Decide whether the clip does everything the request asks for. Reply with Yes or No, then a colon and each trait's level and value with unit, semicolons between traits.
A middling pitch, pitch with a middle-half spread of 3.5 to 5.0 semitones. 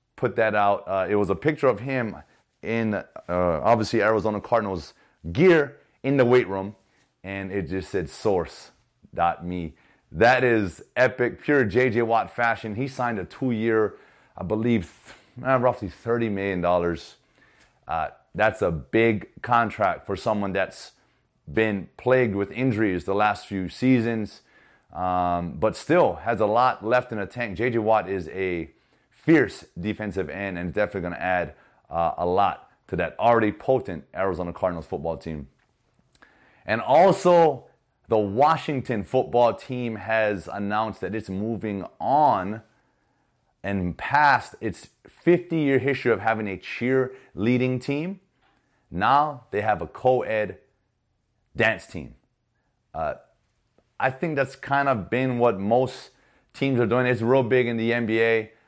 No: low, 110 Hz; average, 4.3 semitones